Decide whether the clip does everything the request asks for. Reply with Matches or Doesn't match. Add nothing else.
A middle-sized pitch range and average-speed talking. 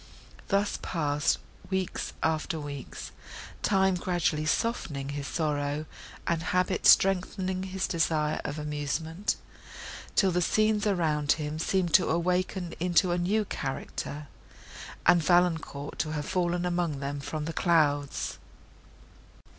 Doesn't match